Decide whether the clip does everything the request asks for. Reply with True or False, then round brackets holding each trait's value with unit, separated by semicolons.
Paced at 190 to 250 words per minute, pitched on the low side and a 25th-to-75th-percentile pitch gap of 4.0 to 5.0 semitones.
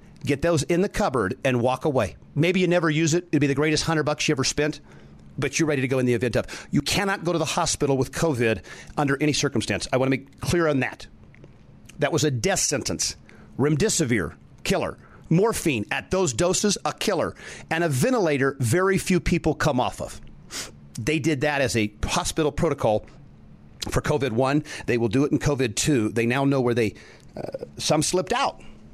False (195 wpm; 145 Hz; 4.6 semitones)